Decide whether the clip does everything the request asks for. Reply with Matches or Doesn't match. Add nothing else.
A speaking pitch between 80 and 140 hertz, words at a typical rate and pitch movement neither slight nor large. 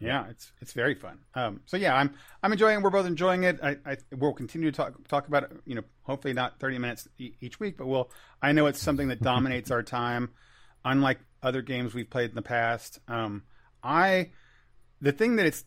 Doesn't match